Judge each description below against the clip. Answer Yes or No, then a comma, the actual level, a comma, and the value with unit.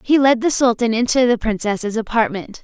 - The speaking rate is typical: Yes, average, 180 wpm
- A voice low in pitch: No, high, 230 Hz